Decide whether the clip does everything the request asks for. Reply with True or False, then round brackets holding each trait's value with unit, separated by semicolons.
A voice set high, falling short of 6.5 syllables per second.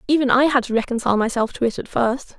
False (245 Hz; 6.7 syllables/s)